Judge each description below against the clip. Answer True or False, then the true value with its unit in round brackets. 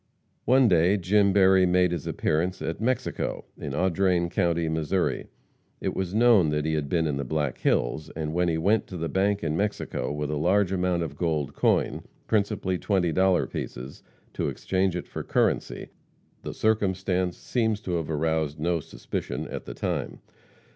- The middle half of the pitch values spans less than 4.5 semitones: True (3.5 semitones)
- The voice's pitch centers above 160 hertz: False (90 Hz)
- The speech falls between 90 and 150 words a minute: False (175 wpm)